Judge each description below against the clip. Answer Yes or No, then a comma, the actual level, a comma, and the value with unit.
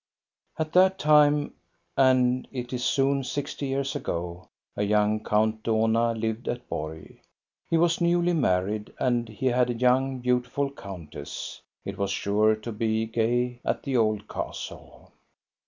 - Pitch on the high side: No, low, 120 Hz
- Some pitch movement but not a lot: Yes, average, 3.9 semitones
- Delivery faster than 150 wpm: No, average, 145 wpm